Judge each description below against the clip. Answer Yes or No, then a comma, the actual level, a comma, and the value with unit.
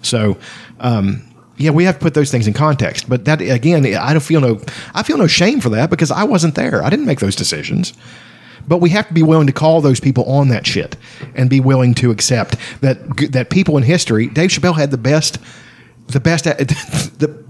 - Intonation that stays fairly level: No, average, 4.4 semitones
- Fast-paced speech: Yes, fast, 225 wpm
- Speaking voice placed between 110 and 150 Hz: Yes, medium, 140 Hz